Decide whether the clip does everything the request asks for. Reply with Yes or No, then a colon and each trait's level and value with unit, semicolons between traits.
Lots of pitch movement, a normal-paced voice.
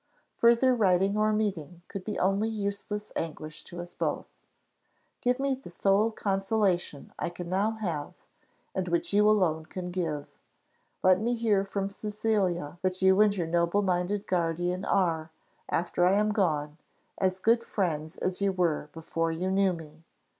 No: average, 3.3 semitones; average, 160 wpm